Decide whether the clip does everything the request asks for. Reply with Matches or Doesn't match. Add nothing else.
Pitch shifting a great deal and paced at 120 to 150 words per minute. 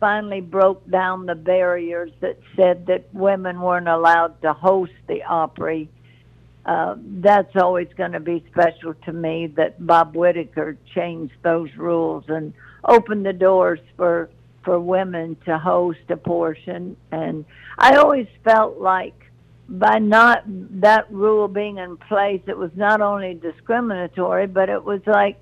Doesn't match